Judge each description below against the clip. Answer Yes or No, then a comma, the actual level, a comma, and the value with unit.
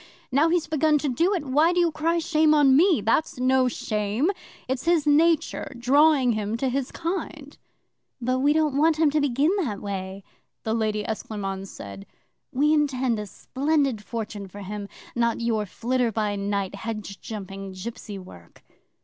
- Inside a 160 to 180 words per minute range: Yes, average, 165 wpm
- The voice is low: No, very high, 255 Hz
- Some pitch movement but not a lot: No, wide, 6.4 semitones